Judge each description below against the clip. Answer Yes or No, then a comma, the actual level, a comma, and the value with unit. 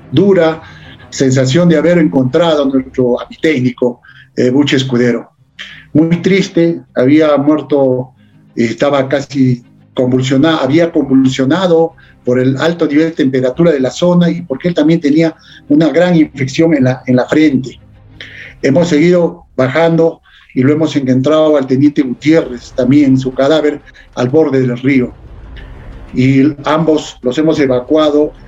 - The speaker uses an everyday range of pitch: Yes, average, 3.6 semitones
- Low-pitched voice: No, medium, 145 Hz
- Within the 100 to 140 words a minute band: Yes, average, 135 wpm